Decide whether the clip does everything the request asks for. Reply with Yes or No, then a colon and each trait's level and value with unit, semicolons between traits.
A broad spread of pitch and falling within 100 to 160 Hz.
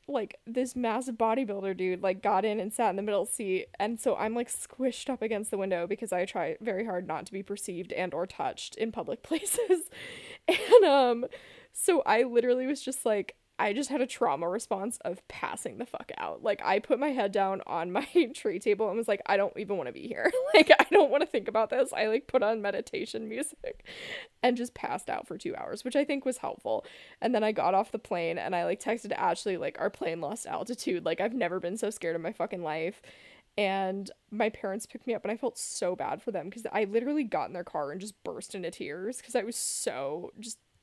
No: wide, 5.7 semitones; high, 230 Hz